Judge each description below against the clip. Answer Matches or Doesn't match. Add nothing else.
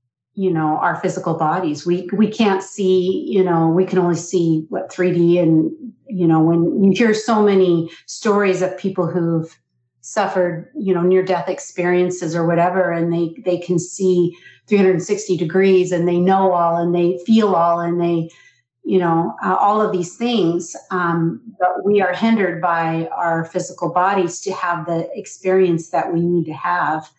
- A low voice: Doesn't match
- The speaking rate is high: Doesn't match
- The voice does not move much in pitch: Matches